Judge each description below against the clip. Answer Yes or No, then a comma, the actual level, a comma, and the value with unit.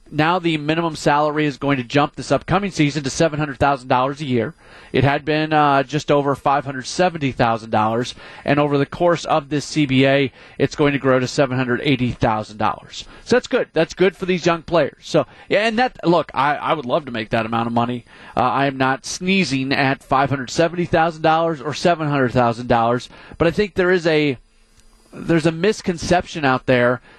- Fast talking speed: Yes, fast, 215 wpm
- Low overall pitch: No, medium, 145 Hz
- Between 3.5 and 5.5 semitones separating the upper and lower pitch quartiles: Yes, average, 4.1 semitones